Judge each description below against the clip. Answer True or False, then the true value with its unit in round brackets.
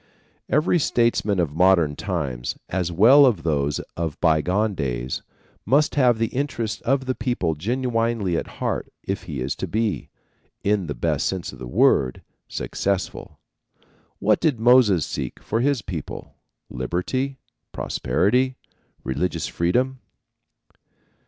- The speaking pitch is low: True (100 Hz)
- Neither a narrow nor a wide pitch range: False (7.3 semitones)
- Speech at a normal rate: False (130 wpm)